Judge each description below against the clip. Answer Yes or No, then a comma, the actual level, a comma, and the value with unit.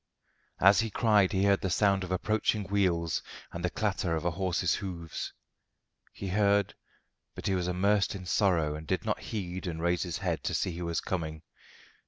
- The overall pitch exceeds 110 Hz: No, very low, 95 Hz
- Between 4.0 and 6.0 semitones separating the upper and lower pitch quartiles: No, average, 2.8 semitones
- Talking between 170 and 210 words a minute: Yes, average, 190 wpm